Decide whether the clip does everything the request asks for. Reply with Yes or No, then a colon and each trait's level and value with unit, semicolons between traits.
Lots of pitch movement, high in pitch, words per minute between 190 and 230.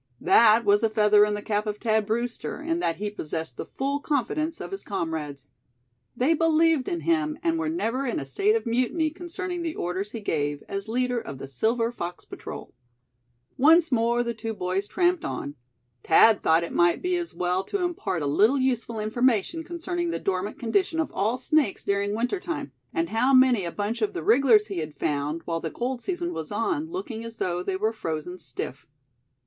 Yes: wide, 8.1 semitones; high, 230 Hz; average, 200 wpm